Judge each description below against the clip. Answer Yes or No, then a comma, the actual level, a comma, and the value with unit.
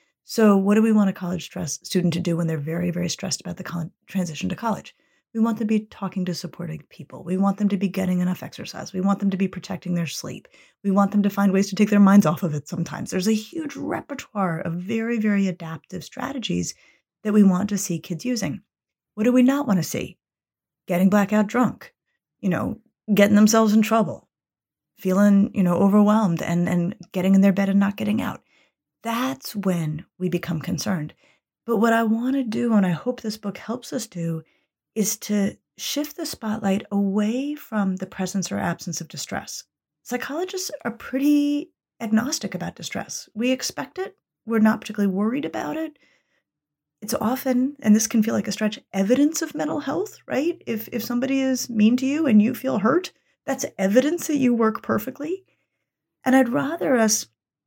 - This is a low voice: No, high, 210 Hz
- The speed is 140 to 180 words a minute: No, average, 195 wpm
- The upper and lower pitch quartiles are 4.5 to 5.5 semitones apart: Yes, average, 5.1 semitones